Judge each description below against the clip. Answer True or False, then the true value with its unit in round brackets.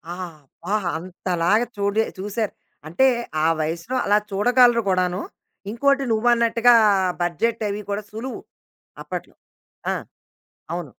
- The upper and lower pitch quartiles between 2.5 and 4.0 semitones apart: False (4.4 semitones)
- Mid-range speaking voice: False (210 Hz)